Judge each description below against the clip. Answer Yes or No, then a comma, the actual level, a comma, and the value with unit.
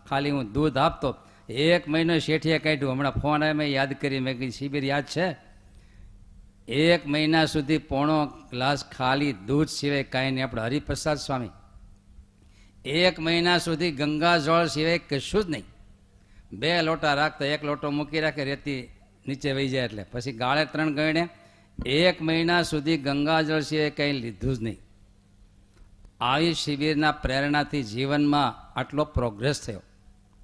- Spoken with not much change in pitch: No, average, 5.3 semitones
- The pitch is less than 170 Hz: Yes, medium, 140 Hz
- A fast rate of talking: Yes, fast, 145 wpm